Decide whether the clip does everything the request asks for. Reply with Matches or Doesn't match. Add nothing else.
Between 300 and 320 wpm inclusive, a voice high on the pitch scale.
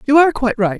Matches